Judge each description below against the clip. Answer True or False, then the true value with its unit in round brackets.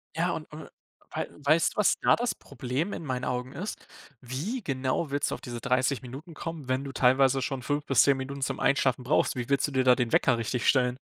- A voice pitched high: False (135 Hz)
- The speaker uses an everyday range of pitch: False (2.2 semitones)